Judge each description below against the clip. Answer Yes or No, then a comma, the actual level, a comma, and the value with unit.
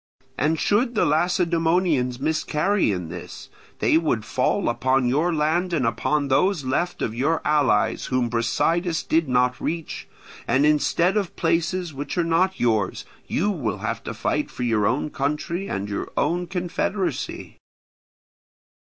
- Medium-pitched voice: Yes, medium, 155 Hz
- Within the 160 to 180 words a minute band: No, average, 145 wpm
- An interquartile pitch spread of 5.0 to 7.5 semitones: Yes, wide, 5.5 semitones